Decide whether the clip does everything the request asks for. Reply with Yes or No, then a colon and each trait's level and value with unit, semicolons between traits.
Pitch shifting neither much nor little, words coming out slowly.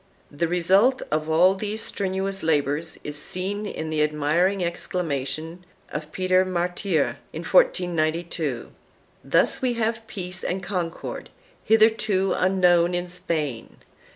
Yes: average, 3.4 semitones; slow, 120 wpm